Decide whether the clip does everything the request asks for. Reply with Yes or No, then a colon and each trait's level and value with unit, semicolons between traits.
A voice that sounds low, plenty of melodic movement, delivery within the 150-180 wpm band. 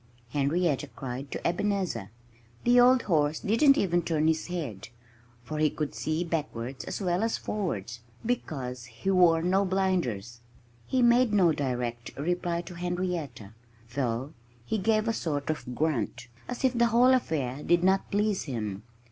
No: medium, 165 Hz; wide, 6.8 semitones; average, 155 wpm